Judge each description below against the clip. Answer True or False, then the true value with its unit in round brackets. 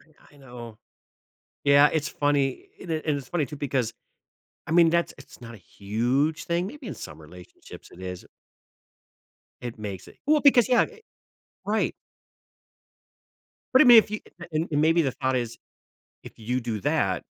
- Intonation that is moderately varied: False (6.4 semitones)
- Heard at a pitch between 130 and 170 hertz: True (140 Hz)